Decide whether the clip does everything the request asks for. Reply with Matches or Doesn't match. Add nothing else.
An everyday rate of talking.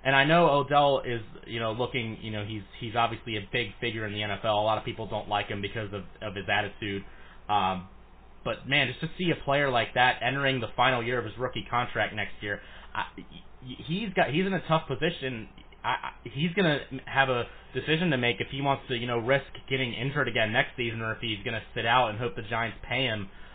Doesn't match